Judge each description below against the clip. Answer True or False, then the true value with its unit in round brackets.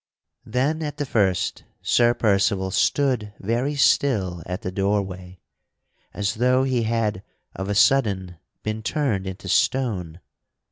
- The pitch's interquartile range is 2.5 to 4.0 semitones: False (5.0 semitones)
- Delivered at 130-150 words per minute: True (135 wpm)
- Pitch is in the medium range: False (105 Hz)